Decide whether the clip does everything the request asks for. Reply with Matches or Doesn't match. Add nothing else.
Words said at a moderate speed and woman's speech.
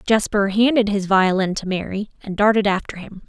Matches